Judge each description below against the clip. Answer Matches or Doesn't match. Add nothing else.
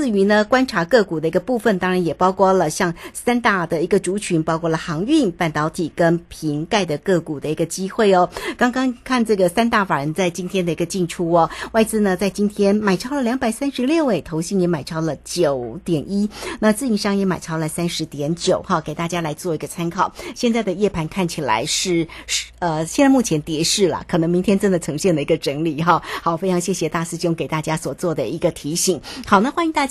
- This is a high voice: Doesn't match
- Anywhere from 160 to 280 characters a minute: Doesn't match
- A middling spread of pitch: Matches